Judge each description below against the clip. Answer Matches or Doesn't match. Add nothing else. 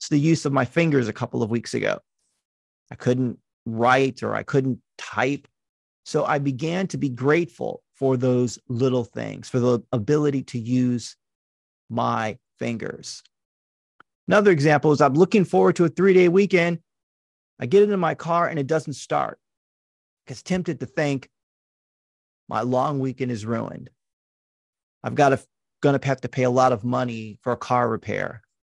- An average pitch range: Matches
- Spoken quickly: Doesn't match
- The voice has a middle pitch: Doesn't match